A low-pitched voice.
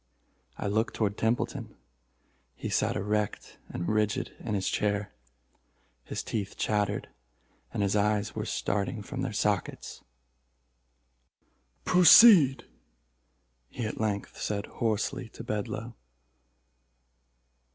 Yes: low, 105 Hz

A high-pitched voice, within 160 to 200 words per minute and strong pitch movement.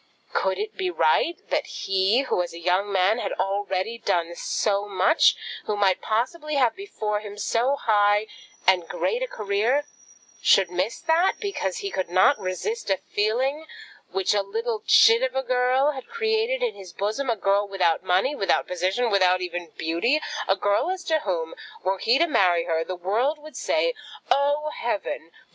Yes: high, 210 Hz; average, 175 wpm; wide, 7.5 semitones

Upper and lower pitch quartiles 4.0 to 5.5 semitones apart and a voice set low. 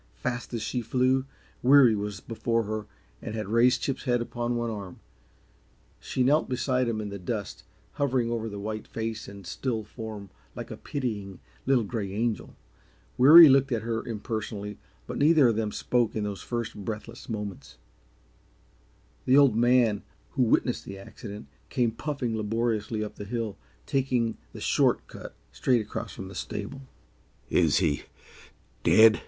No: average, 3.1 semitones; low, 115 Hz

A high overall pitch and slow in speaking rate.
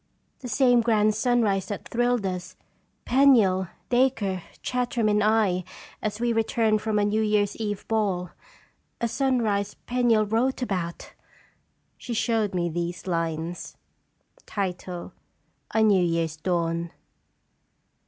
Yes: high, 210 Hz; slow, 125 wpm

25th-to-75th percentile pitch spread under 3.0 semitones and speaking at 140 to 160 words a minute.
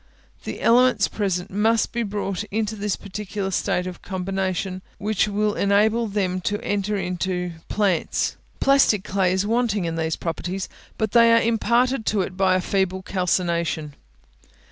Yes: narrow, 2.6 semitones; average, 150 wpm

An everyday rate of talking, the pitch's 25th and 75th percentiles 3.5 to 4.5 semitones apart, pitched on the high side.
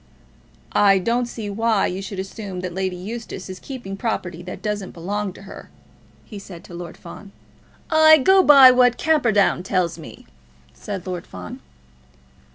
Yes: average, 160 wpm; average, 4.1 semitones; high, 195 Hz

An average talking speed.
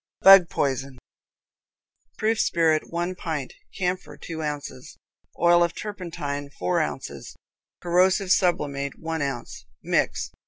No: slow, 110 wpm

